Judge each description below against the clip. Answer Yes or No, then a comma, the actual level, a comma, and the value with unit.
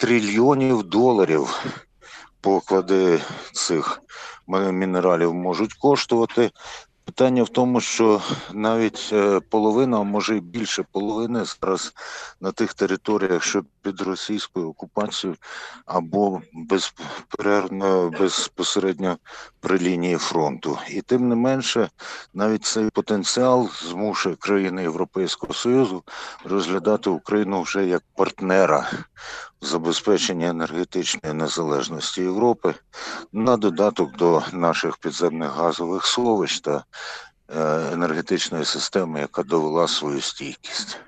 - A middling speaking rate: No, slow, 100 wpm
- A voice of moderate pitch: No, low, 100 Hz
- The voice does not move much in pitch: No, average, 3.1 semitones